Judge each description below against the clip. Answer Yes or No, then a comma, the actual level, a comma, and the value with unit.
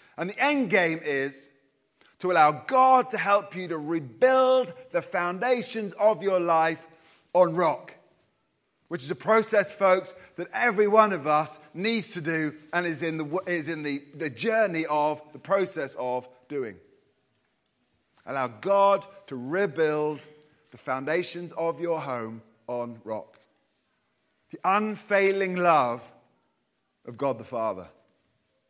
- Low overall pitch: No, medium, 170 Hz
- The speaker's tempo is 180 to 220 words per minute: No, slow, 135 wpm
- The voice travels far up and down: No, average, 4.8 semitones